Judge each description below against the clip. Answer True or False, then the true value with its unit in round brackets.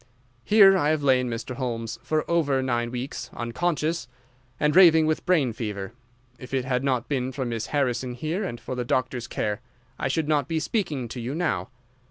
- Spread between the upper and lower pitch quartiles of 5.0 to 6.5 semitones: False (4.3 semitones)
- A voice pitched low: True (130 Hz)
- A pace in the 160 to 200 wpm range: True (190 wpm)